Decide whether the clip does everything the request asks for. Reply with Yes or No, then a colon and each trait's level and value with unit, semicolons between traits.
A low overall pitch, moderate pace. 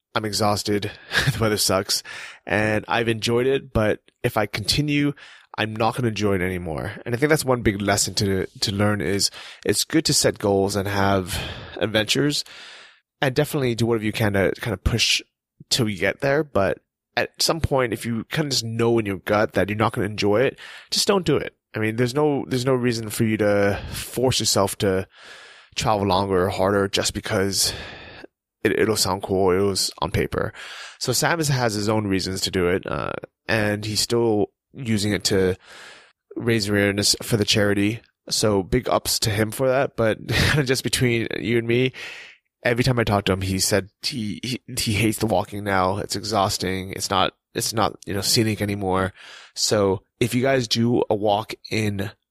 Yes: low, 110 Hz; average, 195 wpm